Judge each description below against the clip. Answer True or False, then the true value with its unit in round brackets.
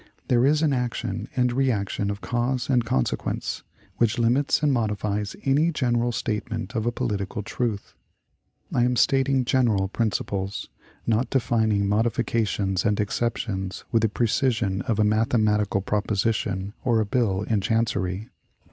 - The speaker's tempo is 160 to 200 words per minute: False (140 wpm)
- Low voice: True (115 Hz)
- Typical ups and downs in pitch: True (3.1 semitones)